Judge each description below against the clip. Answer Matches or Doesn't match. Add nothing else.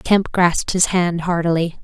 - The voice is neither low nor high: Matches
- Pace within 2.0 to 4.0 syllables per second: Doesn't match